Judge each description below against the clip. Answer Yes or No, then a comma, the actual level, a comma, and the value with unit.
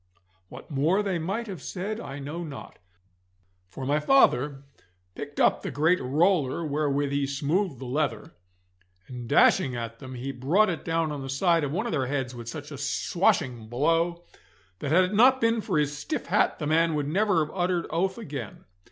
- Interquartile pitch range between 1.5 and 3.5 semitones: No, average, 4.5 semitones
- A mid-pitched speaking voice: Yes, medium, 150 Hz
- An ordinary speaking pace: Yes, average, 190 wpm